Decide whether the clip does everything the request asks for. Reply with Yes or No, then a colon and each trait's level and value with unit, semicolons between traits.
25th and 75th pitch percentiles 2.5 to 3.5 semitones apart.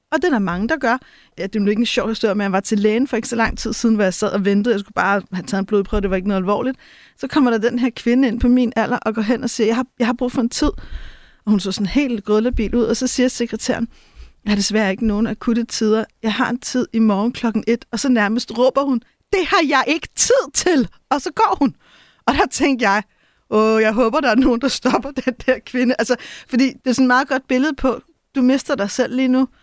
Yes: average, 3.1 semitones